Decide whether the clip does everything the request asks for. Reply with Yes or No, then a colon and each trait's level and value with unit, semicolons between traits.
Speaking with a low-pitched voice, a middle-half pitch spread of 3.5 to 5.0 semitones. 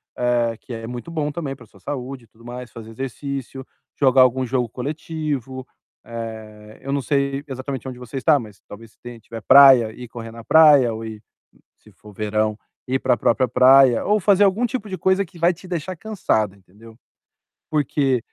Yes: low, 130 Hz; average, 4.2 semitones